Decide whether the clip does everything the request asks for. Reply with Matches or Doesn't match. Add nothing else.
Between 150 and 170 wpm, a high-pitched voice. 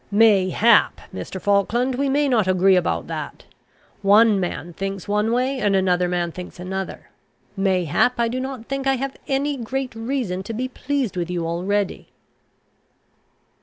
Matches